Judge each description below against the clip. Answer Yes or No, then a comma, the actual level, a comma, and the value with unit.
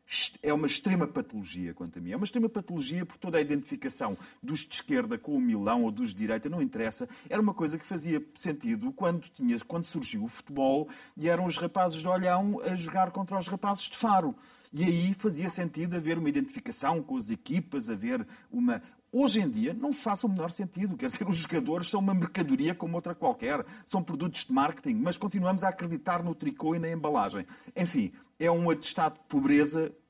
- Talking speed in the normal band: No, fast, 200 wpm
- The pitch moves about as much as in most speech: No, wide, 6.7 semitones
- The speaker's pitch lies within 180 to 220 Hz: Yes, high, 190 Hz